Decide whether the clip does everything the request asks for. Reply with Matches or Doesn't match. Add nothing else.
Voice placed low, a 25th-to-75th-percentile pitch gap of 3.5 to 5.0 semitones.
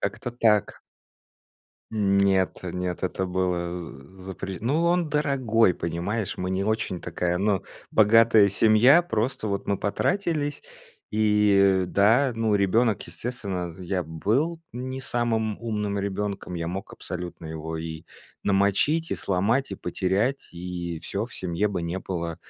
Matches